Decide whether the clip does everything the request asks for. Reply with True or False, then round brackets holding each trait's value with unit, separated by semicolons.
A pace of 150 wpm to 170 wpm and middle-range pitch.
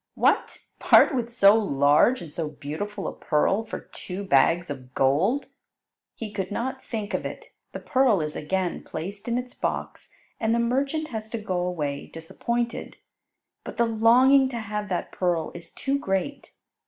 False (165 wpm; 205 Hz)